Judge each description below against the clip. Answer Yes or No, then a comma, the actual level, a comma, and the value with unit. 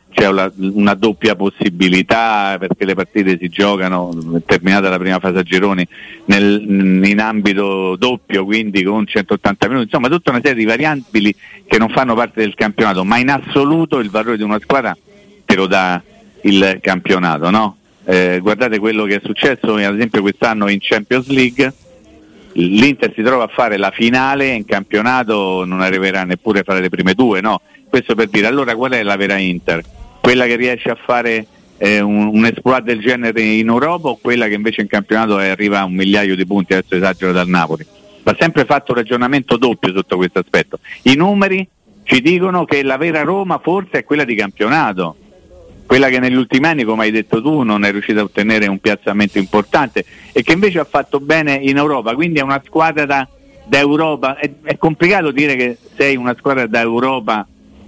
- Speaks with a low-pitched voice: Yes, low, 110 Hz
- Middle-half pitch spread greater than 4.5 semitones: Yes, average, 5.2 semitones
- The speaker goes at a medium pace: No, fast, 185 wpm